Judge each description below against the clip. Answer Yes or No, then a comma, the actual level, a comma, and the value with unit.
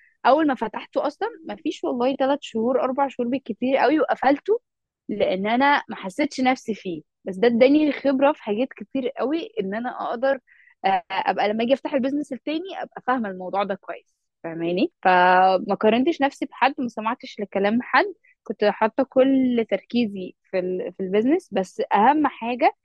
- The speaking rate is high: Yes, fast, 160 wpm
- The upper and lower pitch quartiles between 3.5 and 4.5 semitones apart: No, wide, 5.4 semitones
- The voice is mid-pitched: No, very high, 255 Hz